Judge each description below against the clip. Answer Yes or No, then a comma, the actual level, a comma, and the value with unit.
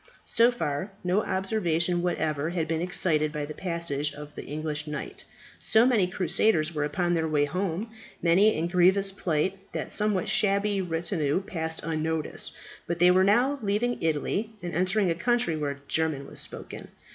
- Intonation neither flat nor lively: Yes, average, 4.0 semitones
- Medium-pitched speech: Yes, medium, 175 Hz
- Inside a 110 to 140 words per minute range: No, average, 170 wpm